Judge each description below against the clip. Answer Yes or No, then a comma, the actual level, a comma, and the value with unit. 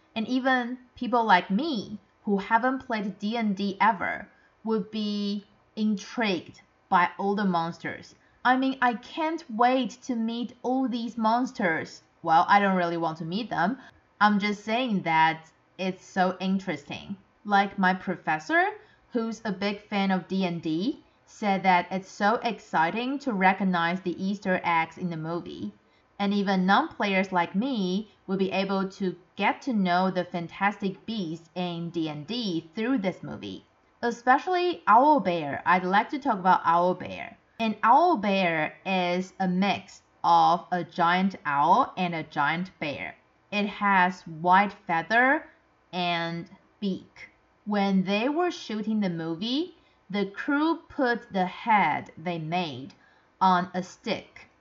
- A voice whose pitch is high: Yes, high, 195 Hz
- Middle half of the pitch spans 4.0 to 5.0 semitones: Yes, average, 4.3 semitones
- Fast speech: No, average, 145 wpm